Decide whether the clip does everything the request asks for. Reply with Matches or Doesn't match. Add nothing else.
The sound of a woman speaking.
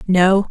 Matches